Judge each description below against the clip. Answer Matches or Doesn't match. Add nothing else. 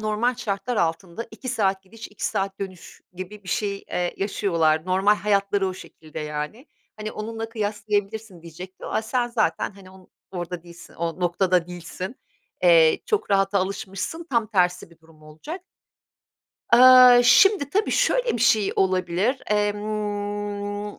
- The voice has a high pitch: Matches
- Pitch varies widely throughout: Doesn't match